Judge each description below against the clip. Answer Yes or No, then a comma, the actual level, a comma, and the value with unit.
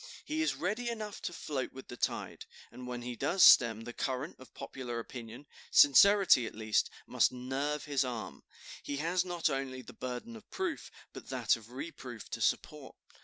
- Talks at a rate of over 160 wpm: Yes, average, 180 wpm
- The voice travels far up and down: Yes, wide, 6.6 semitones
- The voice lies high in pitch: No, low, 135 Hz